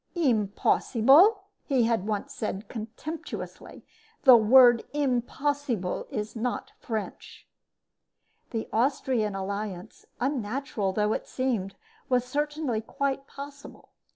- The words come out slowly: Yes, slow, 95 wpm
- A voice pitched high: Yes, high, 245 Hz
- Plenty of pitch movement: No, average, 4.5 semitones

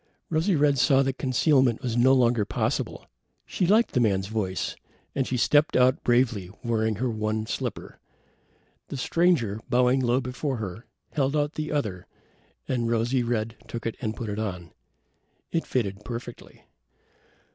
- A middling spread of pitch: Yes, average, 3.5 semitones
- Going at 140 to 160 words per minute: Yes, average, 155 wpm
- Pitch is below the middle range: Yes, low, 120 Hz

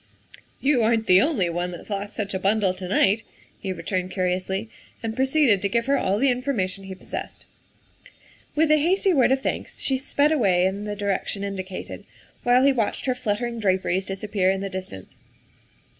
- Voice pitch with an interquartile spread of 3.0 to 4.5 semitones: No, average, 5.0 semitones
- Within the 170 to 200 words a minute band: Yes, average, 185 wpm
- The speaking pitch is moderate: No, high, 205 Hz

